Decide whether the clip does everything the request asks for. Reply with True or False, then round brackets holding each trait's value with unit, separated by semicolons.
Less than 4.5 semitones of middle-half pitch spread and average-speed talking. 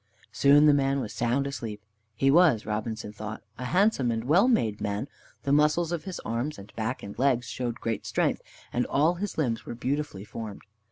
False (5.0 semitones; 190 wpm)